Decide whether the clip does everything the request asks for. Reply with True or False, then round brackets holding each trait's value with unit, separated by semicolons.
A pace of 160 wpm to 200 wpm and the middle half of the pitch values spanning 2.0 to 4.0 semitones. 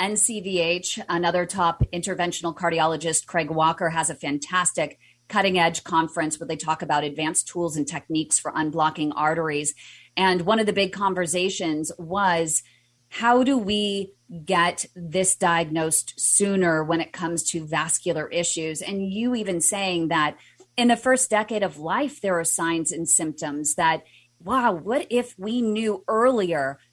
False (150 wpm; 3.6 semitones)